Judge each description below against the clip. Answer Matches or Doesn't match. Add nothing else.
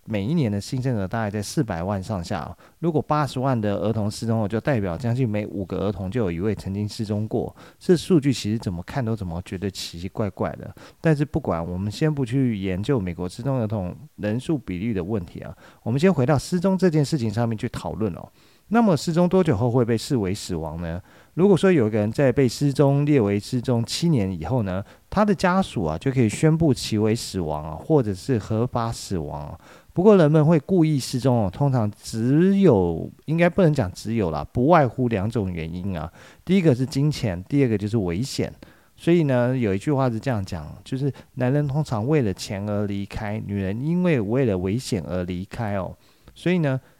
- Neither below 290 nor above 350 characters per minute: Matches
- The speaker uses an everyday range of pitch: Doesn't match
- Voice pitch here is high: Doesn't match